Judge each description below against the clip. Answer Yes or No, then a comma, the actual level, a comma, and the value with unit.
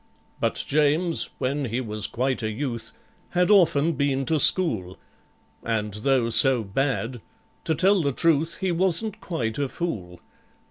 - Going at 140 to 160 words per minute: Yes, average, 145 wpm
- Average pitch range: No, wide, 6.4 semitones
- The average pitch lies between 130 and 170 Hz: Yes, low, 135 Hz